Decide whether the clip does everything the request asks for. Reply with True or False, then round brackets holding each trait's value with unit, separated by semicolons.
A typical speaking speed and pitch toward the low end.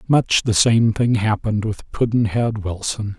True (150 wpm; 110 Hz)